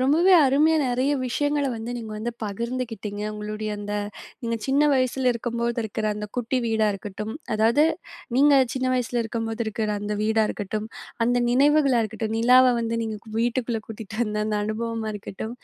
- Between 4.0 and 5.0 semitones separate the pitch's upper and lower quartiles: No, average, 2.8 semitones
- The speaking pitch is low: No, high, 230 Hz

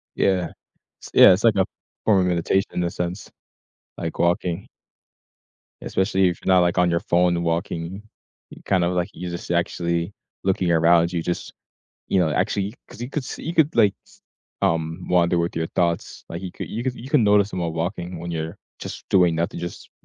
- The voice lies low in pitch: Yes, very low, 90 Hz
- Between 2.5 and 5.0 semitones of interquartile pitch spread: No, narrow, 2.1 semitones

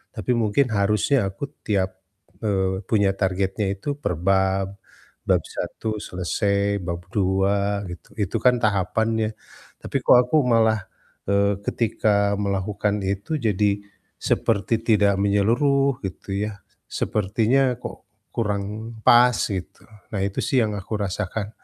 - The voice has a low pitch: Yes, low, 100 Hz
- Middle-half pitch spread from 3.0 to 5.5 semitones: No, narrow, 2.4 semitones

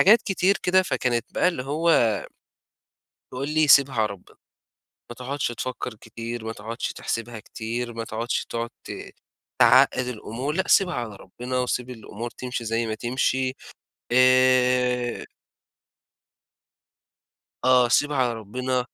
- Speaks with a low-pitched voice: Yes, low, 125 Hz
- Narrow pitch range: Yes, narrow, 2.1 semitones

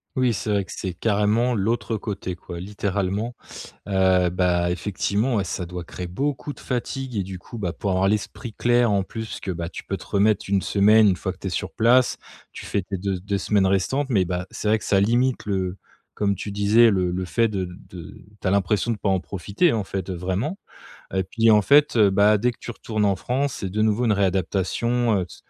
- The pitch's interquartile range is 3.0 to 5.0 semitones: Yes, average, 3.3 semitones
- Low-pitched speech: Yes, low, 100 Hz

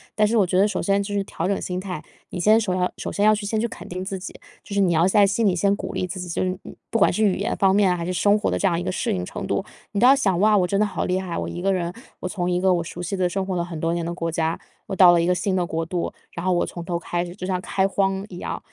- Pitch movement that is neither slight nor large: No, narrow, 2.3 semitones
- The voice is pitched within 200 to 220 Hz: No, medium, 185 Hz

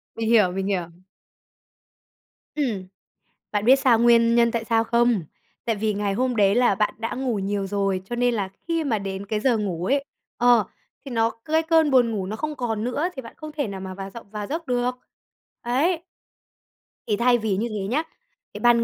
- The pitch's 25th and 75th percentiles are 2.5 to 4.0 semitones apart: Yes, average, 3.6 semitones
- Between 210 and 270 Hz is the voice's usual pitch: Yes, high, 230 Hz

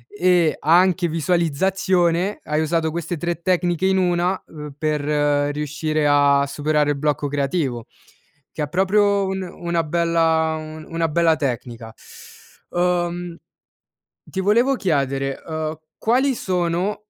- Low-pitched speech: No, medium, 165 Hz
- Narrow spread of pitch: No, average, 3.1 semitones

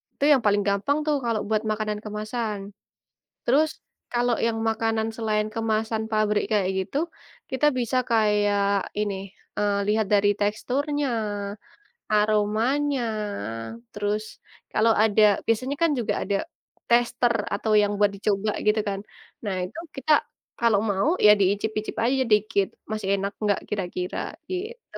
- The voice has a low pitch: No, high, 215 Hz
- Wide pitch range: No, narrow, 2.5 semitones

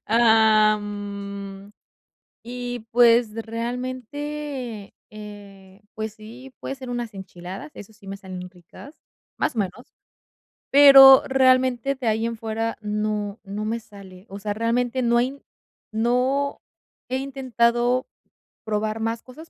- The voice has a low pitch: No, high, 225 Hz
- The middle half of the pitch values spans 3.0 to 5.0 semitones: Yes, average, 3.3 semitones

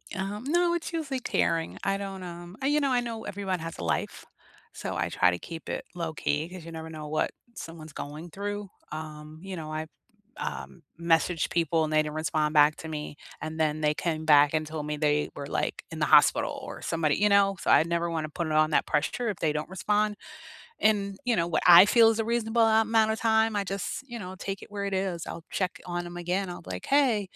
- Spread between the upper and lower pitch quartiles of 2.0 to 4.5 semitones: No, average, 4.9 semitones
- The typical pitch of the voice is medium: Yes, medium, 175 Hz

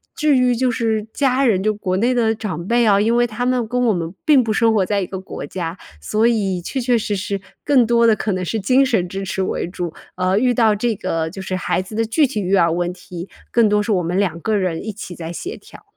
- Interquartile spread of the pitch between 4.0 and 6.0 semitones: Yes, average, 4.4 semitones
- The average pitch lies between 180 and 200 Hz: No, high, 210 Hz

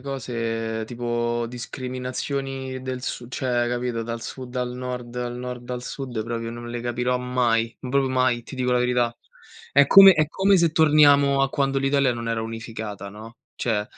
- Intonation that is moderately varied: No, narrow, 2.0 semitones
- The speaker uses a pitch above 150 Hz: No, low, 125 Hz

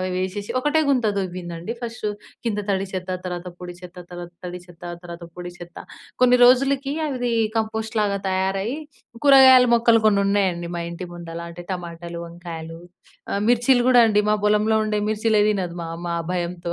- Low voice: No, high, 195 Hz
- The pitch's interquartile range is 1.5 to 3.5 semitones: No, average, 4.6 semitones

